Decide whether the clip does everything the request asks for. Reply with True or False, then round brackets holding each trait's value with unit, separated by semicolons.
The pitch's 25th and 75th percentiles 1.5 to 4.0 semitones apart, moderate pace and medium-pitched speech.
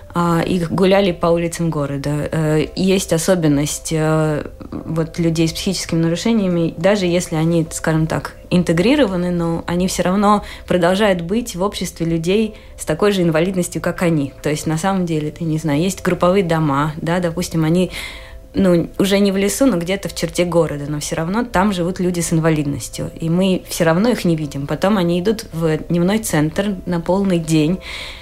False (2.7 semitones; 170 wpm; 170 Hz)